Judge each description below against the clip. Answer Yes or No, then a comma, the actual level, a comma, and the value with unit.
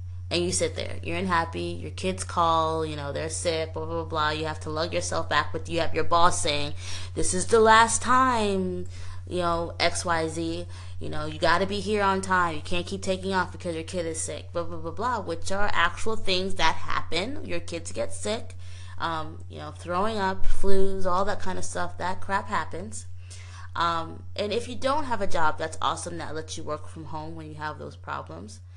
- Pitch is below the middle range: Yes, very low, 90 Hz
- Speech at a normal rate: No, fast, 220 wpm